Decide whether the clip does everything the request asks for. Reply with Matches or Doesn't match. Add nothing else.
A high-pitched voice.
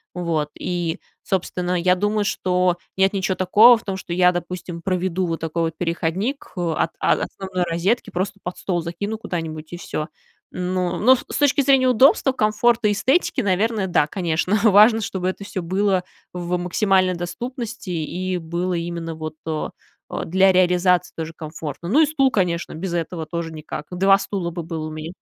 Doesn't match